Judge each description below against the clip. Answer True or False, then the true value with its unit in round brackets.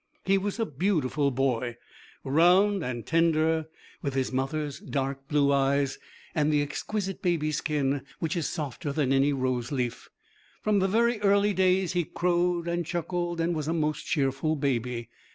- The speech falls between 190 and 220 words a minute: False (155 wpm)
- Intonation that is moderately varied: True (4.4 semitones)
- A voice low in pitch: False (155 Hz)